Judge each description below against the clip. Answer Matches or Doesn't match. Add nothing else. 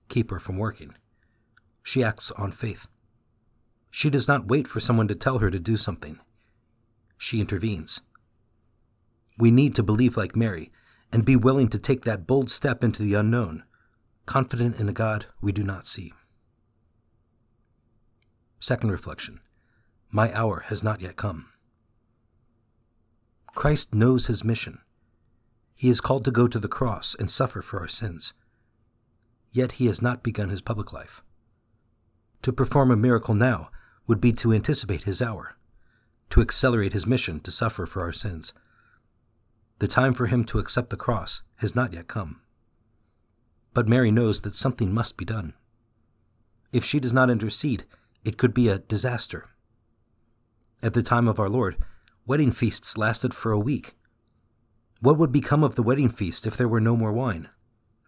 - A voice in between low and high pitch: Doesn't match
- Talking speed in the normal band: Matches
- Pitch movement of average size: Doesn't match